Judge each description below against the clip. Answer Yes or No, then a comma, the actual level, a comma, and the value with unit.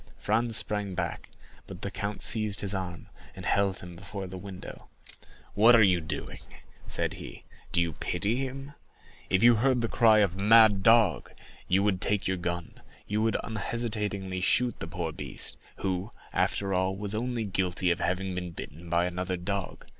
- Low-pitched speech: Yes, low, 100 Hz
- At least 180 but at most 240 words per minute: No, average, 170 wpm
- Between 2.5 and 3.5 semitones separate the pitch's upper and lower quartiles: Yes, average, 3.1 semitones